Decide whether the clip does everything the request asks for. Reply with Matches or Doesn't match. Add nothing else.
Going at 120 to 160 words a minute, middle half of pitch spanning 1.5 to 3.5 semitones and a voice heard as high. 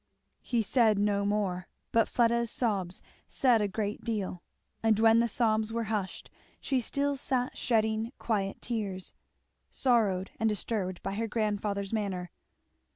Matches